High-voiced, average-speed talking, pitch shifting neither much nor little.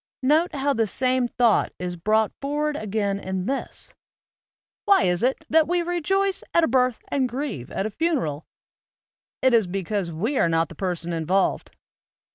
No: high, 235 Hz; average, 170 wpm; wide, 7.7 semitones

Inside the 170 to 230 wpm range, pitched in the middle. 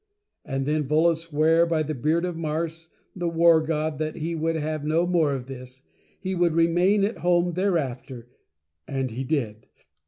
Yes: average, 185 wpm; medium, 160 Hz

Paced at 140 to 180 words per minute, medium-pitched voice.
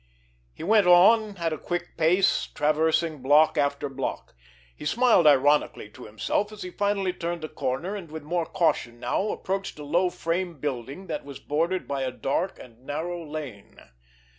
Yes: average, 170 wpm; medium, 160 Hz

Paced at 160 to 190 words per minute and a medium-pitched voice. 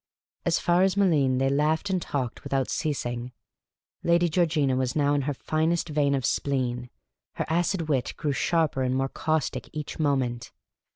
Yes: average, 165 wpm; medium, 145 Hz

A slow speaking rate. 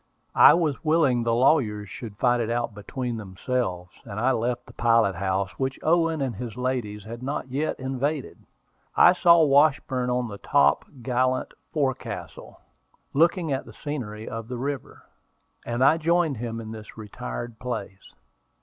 No: average, 160 wpm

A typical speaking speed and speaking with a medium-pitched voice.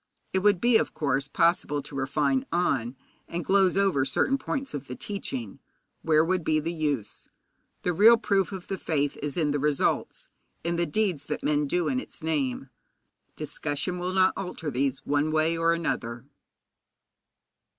Yes: average, 170 wpm; medium, 160 Hz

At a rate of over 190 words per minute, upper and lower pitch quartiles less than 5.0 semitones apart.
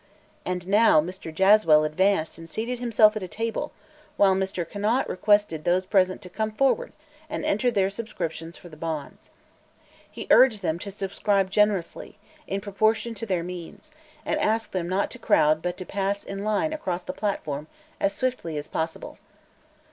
No: average, 170 wpm; average, 3.7 semitones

